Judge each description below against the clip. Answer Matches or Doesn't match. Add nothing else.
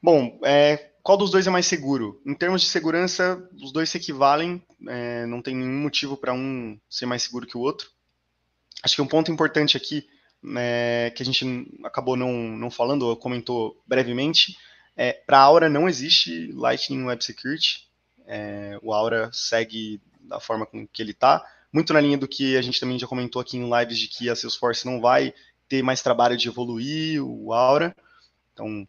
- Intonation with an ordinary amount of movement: Matches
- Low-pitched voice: Matches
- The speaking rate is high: Matches